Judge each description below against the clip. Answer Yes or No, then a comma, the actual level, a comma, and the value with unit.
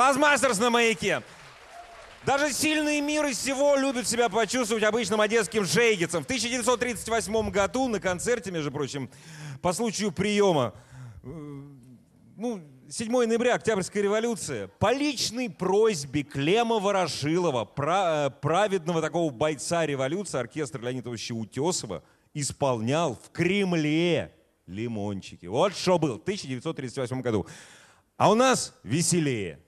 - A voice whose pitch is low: No, medium, 175 Hz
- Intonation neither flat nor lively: No, wide, 8.4 semitones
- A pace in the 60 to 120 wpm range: Yes, slow, 110 wpm